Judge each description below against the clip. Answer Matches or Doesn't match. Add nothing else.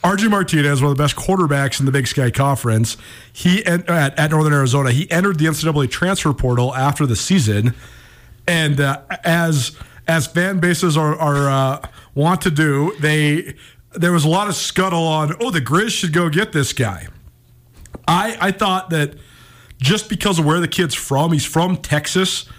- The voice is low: Doesn't match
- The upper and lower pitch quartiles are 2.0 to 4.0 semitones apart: Doesn't match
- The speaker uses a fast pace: Doesn't match